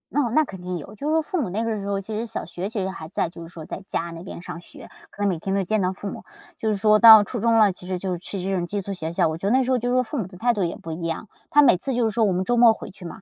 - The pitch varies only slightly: No, average, 4.2 semitones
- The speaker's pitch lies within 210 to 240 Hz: No, high, 200 Hz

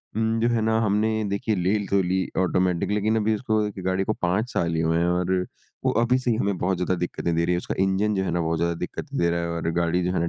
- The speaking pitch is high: No, very low, 95 Hz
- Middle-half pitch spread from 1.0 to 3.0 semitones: No, average, 3.8 semitones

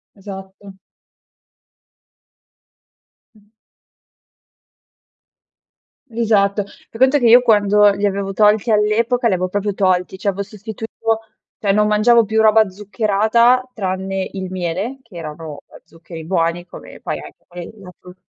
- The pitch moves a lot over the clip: No, average, 2.8 semitones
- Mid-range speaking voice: No, high, 205 Hz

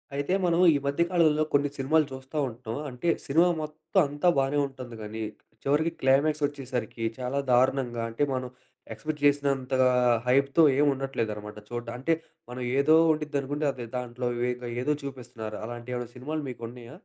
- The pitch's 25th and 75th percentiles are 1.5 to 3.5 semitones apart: Yes, average, 3.1 semitones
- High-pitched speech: No, low, 135 Hz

